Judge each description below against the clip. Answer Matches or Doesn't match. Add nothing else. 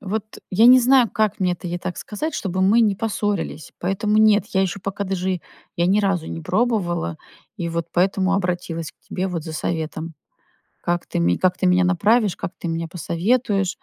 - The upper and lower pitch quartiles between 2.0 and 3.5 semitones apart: Matches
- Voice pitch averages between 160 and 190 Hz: Matches